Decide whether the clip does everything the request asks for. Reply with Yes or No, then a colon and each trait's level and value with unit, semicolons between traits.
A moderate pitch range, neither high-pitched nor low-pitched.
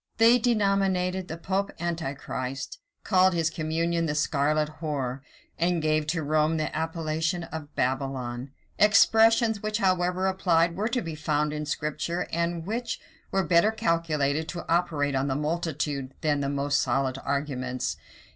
Yes: average, 3.8 semitones; medium, 160 Hz